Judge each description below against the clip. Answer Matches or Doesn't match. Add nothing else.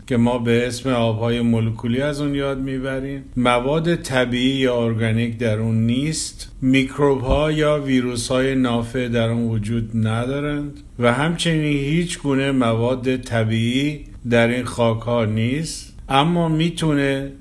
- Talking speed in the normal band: Matches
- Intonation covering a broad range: Doesn't match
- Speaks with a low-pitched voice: Matches